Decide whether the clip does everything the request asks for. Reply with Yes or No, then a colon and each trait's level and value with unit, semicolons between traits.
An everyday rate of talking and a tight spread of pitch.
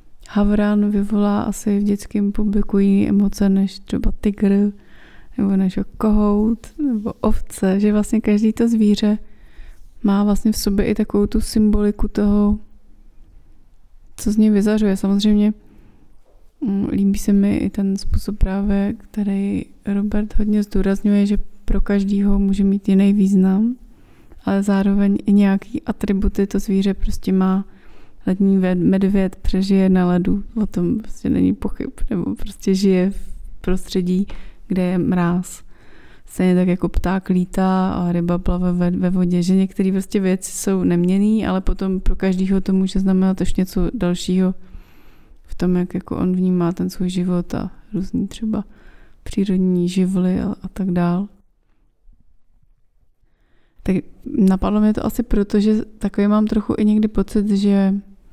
Yes: average, 140 wpm; narrow, 1.8 semitones